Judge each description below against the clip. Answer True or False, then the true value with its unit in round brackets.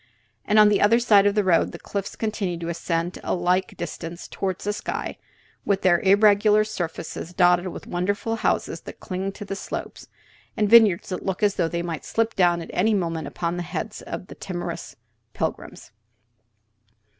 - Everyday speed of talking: True (175 wpm)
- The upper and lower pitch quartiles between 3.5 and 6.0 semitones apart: False (3.1 semitones)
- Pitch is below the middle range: False (190 Hz)